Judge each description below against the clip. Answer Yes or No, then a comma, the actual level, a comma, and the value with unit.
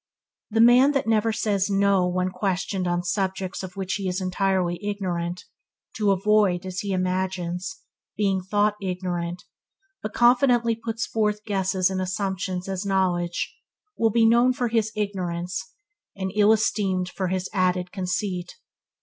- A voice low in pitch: No, high, 190 Hz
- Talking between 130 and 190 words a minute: Yes, average, 145 wpm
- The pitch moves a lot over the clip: No, narrow, 2.6 semitones